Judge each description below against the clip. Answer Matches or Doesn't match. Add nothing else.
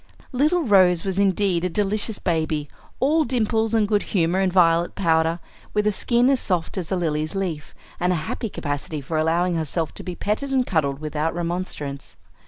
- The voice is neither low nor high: Matches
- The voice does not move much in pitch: Doesn't match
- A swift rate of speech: Doesn't match